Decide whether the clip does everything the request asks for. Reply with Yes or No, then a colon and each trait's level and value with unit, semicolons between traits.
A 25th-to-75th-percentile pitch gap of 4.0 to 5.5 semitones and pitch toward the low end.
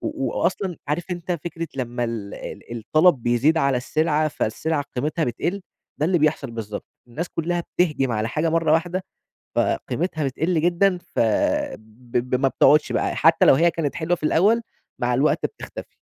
No: average, 5.0 semitones; medium, 155 Hz